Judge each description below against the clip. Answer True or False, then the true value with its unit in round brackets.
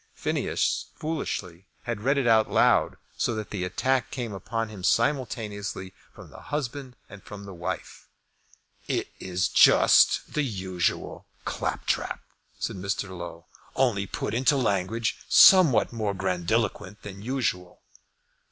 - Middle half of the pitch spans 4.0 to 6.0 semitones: True (4.5 semitones)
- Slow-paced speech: True (130 wpm)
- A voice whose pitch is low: True (105 Hz)